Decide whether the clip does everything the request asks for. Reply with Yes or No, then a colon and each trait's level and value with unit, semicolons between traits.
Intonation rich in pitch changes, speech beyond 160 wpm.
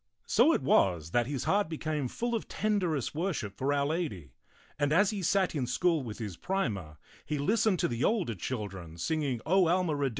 Yes: wide, 8.2 semitones; average, 195 wpm